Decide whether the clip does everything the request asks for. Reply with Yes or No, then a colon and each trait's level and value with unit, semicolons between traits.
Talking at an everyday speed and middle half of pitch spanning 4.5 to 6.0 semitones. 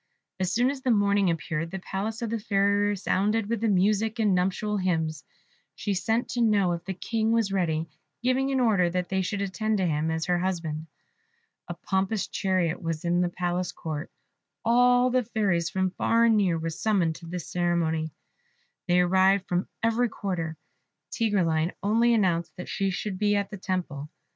No: average, 180 wpm; average, 3.8 semitones